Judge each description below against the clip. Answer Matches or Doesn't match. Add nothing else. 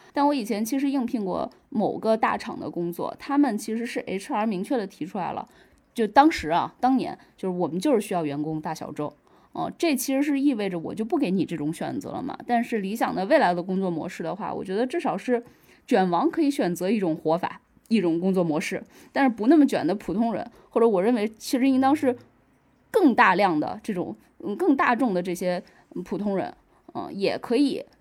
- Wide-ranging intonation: Matches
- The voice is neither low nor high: Doesn't match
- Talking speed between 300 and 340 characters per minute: Matches